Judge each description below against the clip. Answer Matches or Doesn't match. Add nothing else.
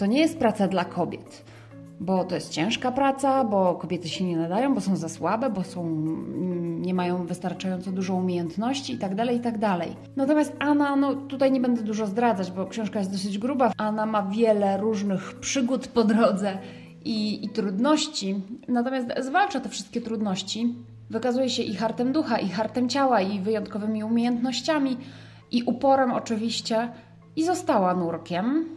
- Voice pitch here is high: Matches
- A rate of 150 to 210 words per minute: Matches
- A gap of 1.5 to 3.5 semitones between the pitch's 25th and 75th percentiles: Doesn't match